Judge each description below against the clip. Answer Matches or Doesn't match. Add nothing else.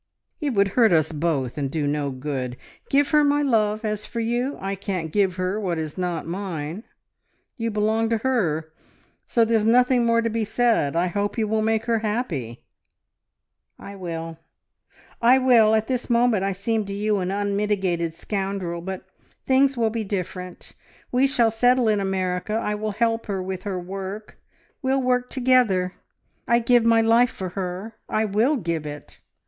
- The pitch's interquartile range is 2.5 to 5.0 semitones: Matches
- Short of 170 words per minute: Doesn't match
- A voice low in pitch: Doesn't match